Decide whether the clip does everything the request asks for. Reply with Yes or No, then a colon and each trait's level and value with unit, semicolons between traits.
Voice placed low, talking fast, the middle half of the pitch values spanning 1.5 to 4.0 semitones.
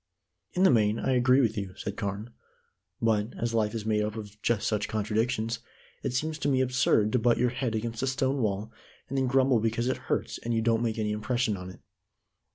Yes: low, 115 Hz; fast, 220 wpm; average, 3.0 semitones